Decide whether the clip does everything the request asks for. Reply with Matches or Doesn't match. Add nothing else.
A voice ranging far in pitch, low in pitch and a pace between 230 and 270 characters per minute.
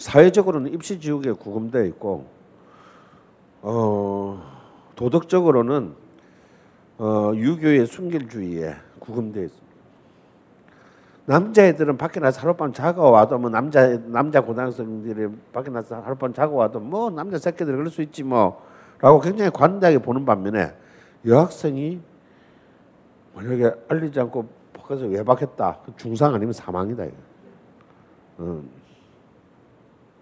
Matches